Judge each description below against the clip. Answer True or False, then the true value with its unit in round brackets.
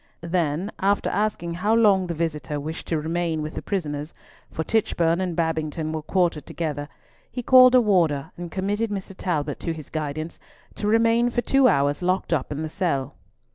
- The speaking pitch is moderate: True (170 Hz)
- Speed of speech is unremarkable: True (175 wpm)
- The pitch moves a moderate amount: True (4.6 semitones)